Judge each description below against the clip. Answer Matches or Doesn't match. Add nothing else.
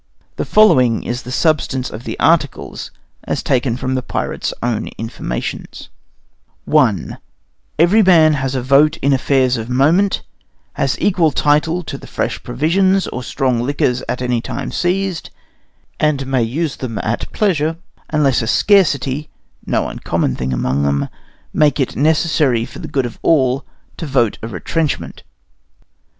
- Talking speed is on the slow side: Doesn't match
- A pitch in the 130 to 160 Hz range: Matches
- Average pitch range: Matches